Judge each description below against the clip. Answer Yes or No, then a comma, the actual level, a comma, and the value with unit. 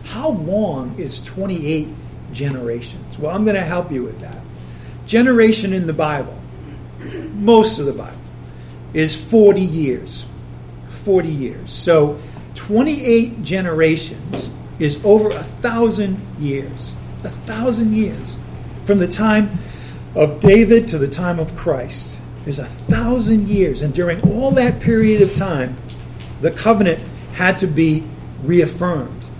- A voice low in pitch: No, medium, 170 Hz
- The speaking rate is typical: No, slow, 130 wpm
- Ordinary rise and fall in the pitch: No, wide, 7.3 semitones